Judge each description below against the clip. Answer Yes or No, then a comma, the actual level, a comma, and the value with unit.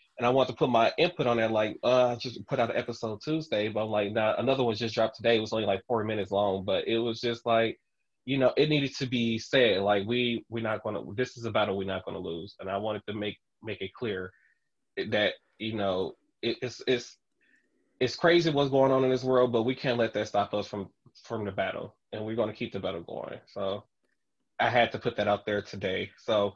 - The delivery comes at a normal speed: No, fast, 255 wpm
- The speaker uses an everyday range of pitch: Yes, average, 3.1 semitones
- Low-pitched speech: Yes, low, 110 Hz